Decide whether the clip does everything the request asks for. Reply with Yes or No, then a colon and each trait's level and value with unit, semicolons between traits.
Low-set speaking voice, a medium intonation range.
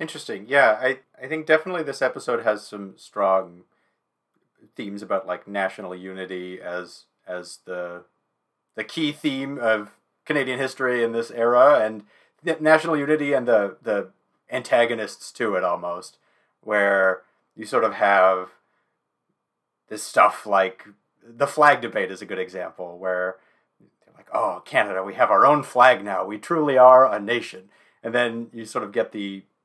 No: low, 105 Hz; wide, 5.8 semitones